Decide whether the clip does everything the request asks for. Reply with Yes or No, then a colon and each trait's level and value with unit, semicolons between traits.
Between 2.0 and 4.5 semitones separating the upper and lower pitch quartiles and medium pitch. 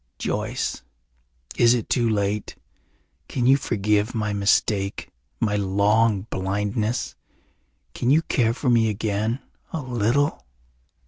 No: average, 2.9 semitones; low, 110 Hz